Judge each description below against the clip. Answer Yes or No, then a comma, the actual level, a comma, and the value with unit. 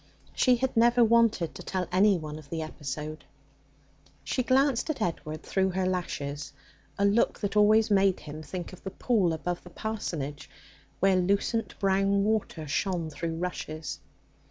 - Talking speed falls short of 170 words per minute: Yes, average, 155 wpm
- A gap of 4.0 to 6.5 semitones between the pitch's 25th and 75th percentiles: Yes, average, 5.1 semitones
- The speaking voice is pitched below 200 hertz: Yes, medium, 185 Hz